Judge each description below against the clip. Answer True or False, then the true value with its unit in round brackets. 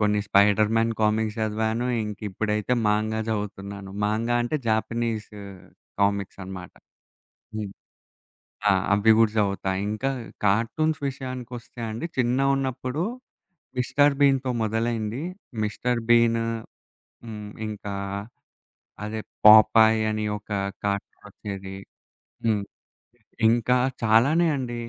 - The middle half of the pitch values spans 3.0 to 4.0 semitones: False (2.4 semitones)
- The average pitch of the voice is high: False (110 Hz)